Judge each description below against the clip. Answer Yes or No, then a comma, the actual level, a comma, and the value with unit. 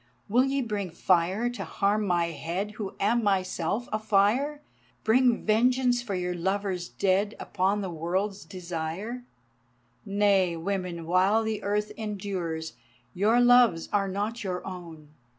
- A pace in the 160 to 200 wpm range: No, slow, 135 wpm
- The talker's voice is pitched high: Yes, high, 200 Hz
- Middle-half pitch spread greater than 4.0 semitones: No, average, 3.4 semitones